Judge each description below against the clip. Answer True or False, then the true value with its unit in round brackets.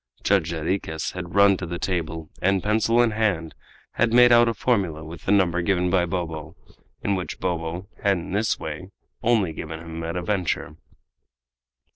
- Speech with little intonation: False (3.5 semitones)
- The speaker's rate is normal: True (175 wpm)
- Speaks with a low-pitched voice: True (90 Hz)